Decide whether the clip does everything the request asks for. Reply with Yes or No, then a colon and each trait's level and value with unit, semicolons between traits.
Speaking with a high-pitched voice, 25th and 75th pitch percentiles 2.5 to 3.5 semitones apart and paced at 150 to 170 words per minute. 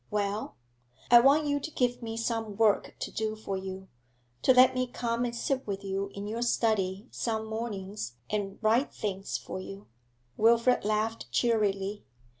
Yes: high, 220 Hz; average, 3.0 semitones; average, 165 wpm